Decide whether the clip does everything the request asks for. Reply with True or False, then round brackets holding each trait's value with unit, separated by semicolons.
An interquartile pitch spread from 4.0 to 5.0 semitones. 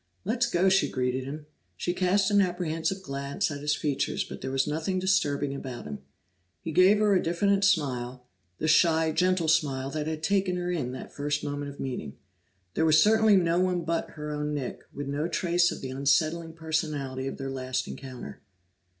True (4.5 semitones)